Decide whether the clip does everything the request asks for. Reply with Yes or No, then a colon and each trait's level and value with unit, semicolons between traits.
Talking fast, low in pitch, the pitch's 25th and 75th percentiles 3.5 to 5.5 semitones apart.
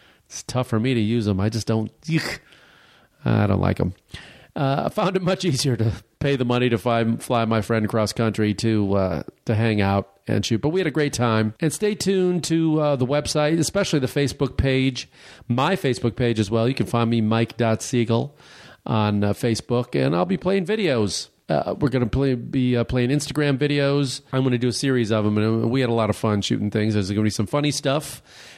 Yes: fast, 225 wpm; low, 120 Hz; average, 4.4 semitones